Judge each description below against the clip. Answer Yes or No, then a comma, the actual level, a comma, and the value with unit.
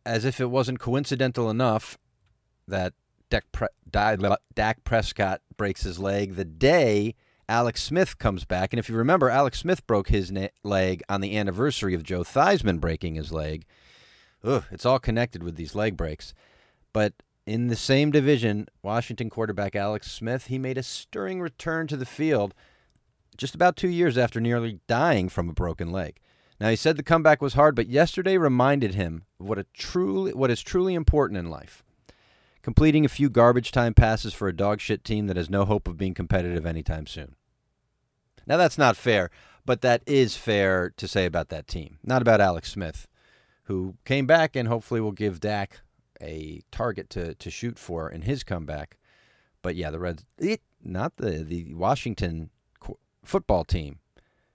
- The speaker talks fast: No, average, 175 wpm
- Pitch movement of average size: No, wide, 6.0 semitones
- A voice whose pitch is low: Yes, low, 105 Hz